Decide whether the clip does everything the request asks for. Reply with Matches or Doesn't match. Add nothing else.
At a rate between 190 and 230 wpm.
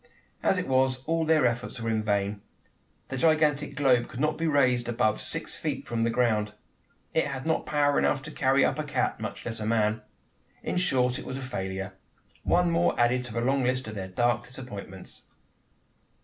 Matches